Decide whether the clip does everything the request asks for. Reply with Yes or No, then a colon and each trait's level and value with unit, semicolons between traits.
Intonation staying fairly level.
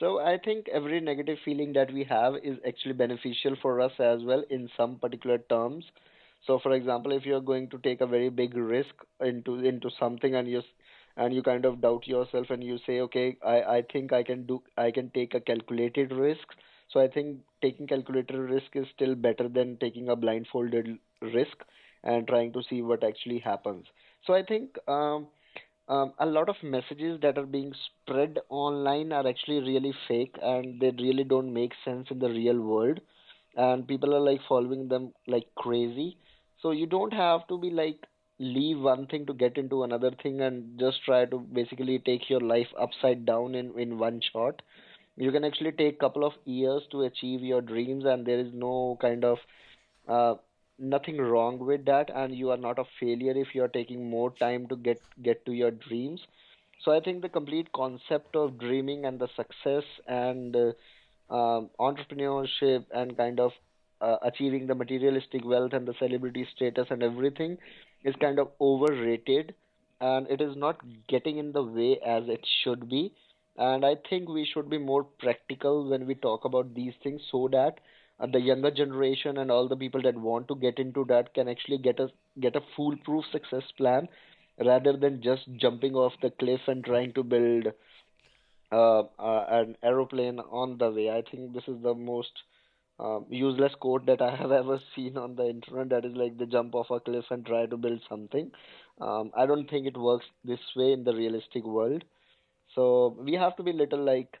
Yes: narrow, 2.3 semitones